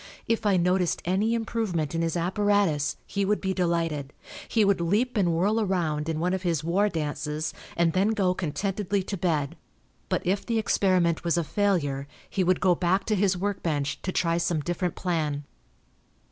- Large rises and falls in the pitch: No, average, 3.3 semitones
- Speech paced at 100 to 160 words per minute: No, average, 185 wpm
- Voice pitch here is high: No, medium, 180 Hz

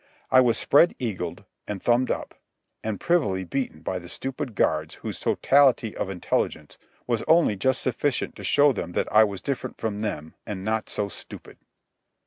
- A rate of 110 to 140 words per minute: No, average, 170 wpm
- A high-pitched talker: No, low, 110 Hz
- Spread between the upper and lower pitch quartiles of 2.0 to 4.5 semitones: No, wide, 5.4 semitones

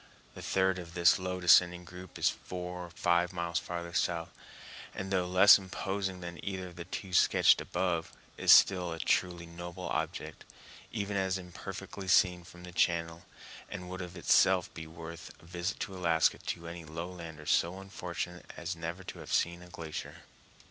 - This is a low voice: Yes, very low, 90 Hz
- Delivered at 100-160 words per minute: No, average, 175 wpm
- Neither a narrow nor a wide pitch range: No, narrow, 1.5 semitones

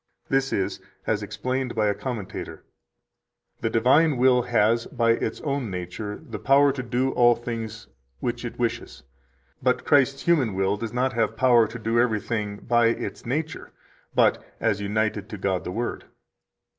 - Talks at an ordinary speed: Yes, average, 160 wpm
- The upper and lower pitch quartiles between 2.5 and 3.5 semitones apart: Yes, average, 3.2 semitones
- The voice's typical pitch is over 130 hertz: No, low, 115 Hz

